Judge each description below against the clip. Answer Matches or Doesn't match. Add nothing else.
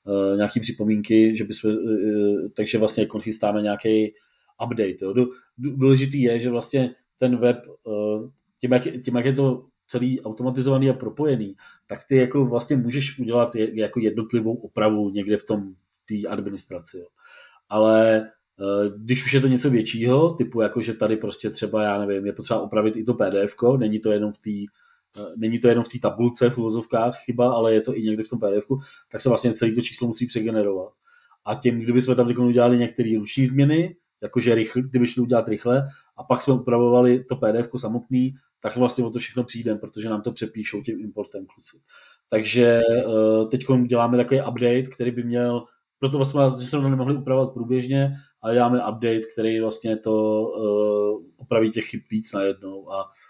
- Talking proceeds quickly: Matches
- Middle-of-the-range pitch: Doesn't match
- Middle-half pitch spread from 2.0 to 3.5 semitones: Matches